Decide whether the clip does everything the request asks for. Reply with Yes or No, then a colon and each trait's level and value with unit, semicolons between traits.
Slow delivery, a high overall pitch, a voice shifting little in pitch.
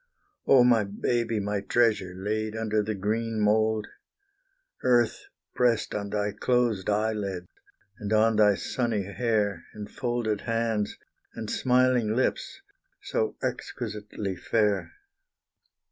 No: slow, 115 wpm; low, 110 Hz; narrow, 2.0 semitones